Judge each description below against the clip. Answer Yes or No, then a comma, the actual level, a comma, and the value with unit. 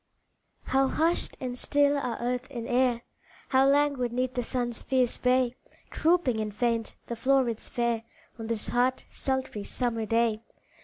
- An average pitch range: No, narrow, 2.1 semitones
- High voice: Yes, high, 245 Hz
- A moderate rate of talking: Yes, average, 150 wpm